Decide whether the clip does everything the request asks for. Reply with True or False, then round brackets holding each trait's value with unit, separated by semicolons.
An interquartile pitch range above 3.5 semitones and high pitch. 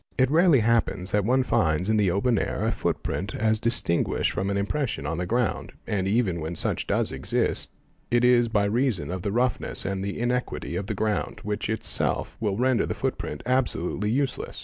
False (3.9 semitones; 110 Hz)